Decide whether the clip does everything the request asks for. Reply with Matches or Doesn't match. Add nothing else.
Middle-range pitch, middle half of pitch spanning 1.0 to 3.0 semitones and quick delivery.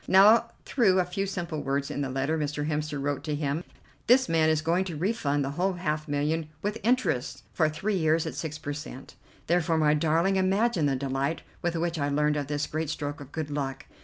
Doesn't match